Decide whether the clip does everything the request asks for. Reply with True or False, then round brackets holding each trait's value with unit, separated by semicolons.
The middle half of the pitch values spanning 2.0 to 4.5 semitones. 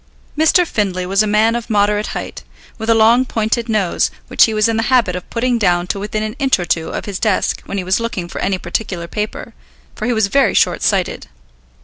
True (3.2 semitones)